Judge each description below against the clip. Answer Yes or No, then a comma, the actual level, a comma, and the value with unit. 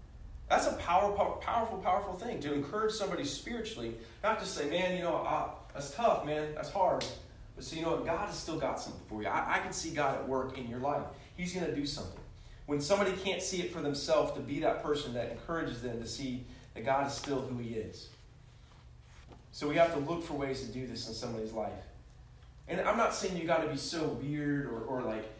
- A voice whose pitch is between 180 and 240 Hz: No, medium, 140 Hz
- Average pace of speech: No, fast, 235 wpm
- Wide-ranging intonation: Yes, wide, 5.8 semitones